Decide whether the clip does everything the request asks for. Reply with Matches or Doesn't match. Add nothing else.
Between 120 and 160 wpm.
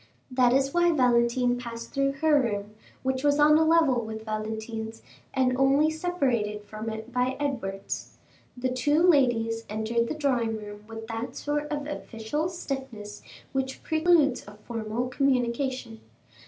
Matches